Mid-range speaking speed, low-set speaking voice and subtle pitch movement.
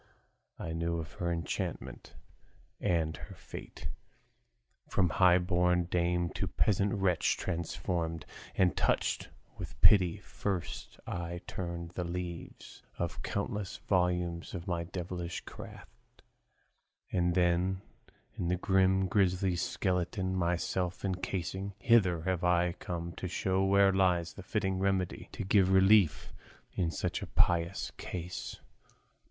No: slow, 125 wpm; very low, 90 Hz; narrow, 1.8 semitones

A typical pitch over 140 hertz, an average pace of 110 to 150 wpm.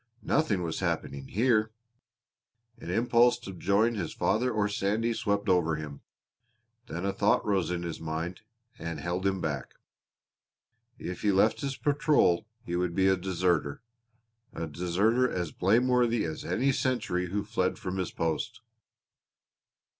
No: very low, 95 Hz; average, 145 wpm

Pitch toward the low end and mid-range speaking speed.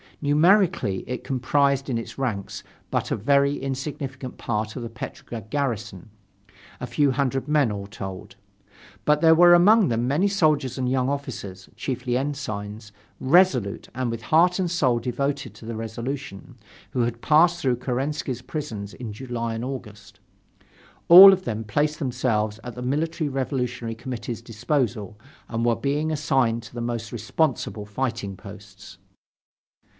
Yes: low, 125 Hz; average, 150 wpm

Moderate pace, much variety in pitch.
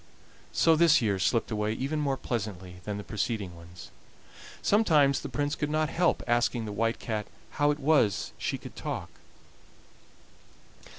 Yes: average, 155 wpm; wide, 5.9 semitones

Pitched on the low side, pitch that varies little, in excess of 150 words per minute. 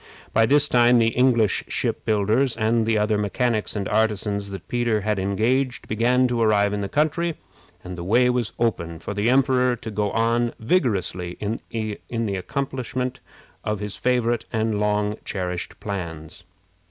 No: low, 110 Hz; average, 3.2 semitones; average, 160 wpm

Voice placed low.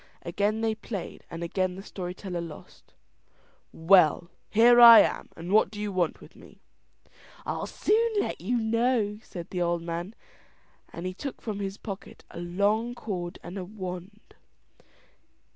No: high, 195 Hz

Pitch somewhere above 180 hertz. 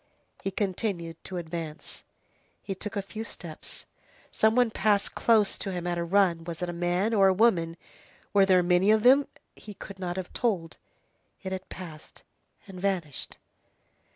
Yes: high, 190 Hz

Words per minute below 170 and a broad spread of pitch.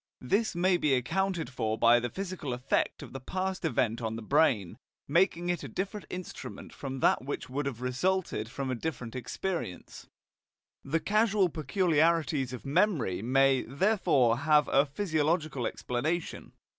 Yes: average, 150 wpm; wide, 6.0 semitones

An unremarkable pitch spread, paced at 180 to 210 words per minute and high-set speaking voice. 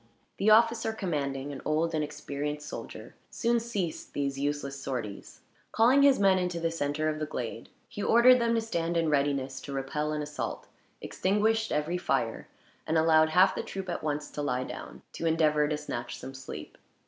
No: average, 5.0 semitones; average, 185 wpm; medium, 155 Hz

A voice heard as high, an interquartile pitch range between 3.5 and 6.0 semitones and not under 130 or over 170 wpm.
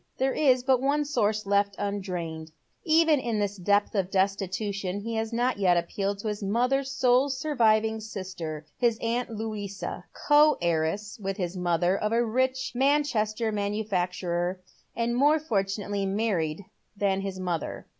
Yes: high, 210 Hz; average, 4.1 semitones; average, 150 wpm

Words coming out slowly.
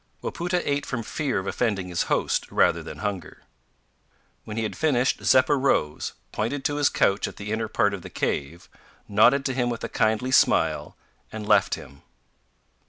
No: average, 175 wpm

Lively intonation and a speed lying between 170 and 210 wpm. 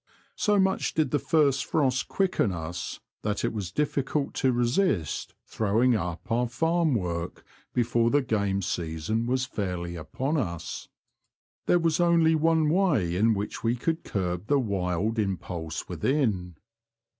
No: wide, 8.7 semitones; average, 145 wpm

